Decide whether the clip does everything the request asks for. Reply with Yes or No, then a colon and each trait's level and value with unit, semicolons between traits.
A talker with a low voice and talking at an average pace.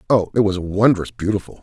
Yes: low, 100 Hz; average, 185 wpm